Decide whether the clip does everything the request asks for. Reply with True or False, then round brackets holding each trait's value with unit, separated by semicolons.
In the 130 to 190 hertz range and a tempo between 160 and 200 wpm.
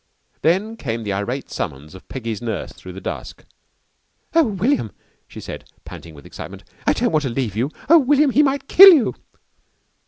True (135 Hz; 180 wpm)